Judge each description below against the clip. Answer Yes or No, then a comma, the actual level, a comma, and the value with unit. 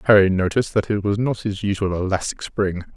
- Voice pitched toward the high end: No, low, 100 Hz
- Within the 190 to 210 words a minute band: Yes, fast, 205 wpm